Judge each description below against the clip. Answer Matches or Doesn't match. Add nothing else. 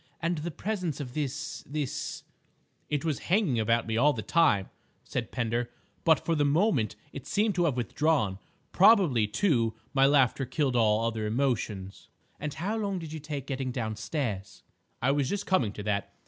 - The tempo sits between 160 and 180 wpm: Matches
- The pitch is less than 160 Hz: Matches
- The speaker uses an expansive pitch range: Matches